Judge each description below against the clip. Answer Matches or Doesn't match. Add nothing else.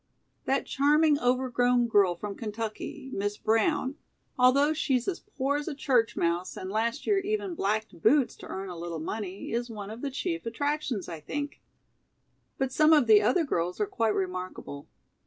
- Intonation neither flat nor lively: Doesn't match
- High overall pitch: Matches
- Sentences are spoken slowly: Doesn't match